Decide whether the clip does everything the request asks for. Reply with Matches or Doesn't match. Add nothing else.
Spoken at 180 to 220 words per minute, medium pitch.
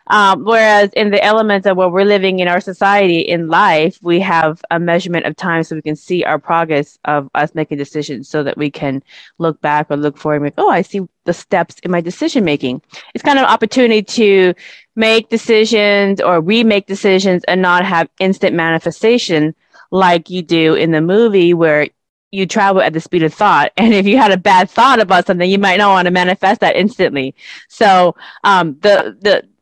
Matches